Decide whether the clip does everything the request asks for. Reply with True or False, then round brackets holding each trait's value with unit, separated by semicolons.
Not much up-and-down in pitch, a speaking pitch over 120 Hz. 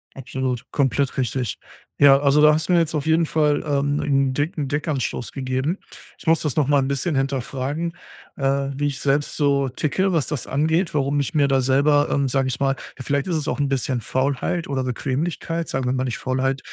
True (2.2 semitones; 140 Hz)